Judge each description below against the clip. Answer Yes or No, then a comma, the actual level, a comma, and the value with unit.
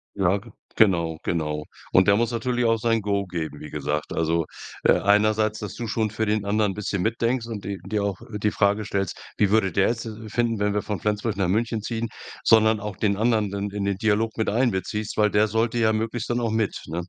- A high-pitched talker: No, low, 105 Hz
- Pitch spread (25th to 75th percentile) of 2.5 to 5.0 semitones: No, narrow, 2.1 semitones